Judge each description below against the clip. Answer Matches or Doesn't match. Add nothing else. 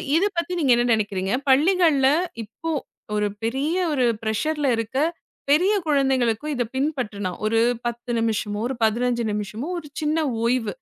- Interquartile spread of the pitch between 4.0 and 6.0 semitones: Matches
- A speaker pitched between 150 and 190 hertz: Doesn't match